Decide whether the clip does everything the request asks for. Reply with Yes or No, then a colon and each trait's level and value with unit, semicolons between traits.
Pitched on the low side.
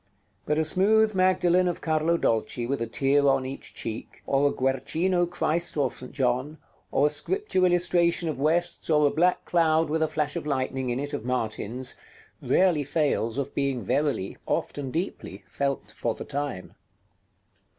No: medium, 145 Hz